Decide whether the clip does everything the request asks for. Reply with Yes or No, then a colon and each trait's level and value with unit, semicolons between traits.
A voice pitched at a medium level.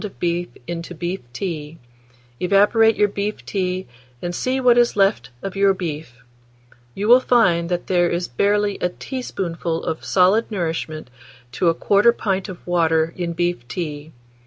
Yes: medium, 180 Hz